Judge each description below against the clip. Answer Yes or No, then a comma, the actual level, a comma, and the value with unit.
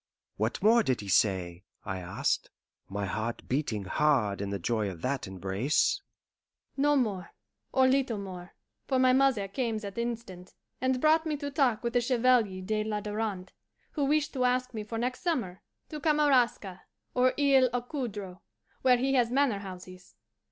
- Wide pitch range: Yes, wide, 6.7 semitones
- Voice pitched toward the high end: Yes, high, 220 Hz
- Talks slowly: No, average, 165 wpm